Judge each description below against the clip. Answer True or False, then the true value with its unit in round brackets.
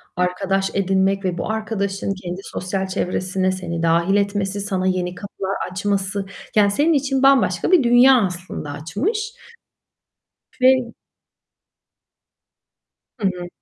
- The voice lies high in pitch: True (195 Hz)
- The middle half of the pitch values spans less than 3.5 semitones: True (2.4 semitones)